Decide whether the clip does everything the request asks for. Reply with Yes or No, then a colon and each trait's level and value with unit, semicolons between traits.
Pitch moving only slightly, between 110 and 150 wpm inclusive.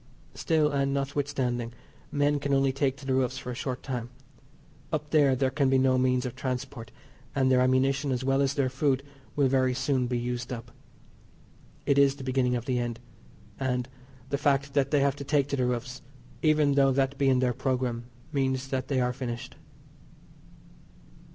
No: narrow, 1.7 semitones; average, 190 wpm